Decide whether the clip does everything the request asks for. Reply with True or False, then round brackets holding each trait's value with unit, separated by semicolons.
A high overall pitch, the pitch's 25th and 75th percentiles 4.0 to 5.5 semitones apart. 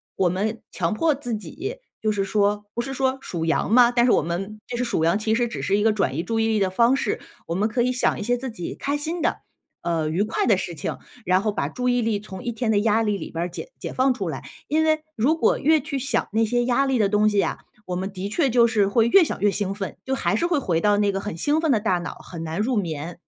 True (215 Hz; 4.5 semitones)